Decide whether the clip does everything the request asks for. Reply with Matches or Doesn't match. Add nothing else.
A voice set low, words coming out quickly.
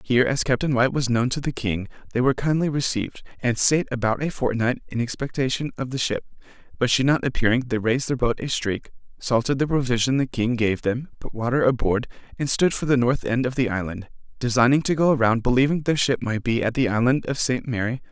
Matches